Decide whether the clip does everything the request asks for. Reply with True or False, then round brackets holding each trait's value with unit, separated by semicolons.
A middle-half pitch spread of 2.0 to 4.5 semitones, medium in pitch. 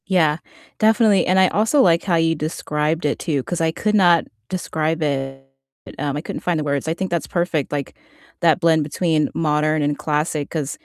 True (2.8 semitones; 160 Hz)